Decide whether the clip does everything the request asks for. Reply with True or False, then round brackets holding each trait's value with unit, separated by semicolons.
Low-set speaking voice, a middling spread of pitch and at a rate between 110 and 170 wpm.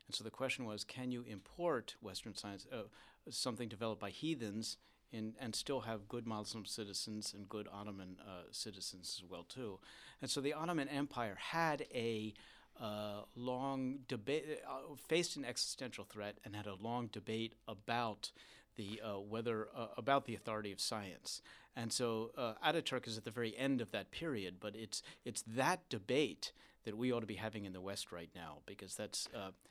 False (110 Hz; 3.4 semitones; 185 wpm)